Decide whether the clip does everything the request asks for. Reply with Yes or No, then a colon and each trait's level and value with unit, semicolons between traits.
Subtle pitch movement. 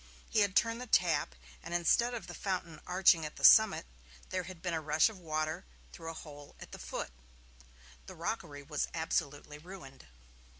No: average, 3.7 semitones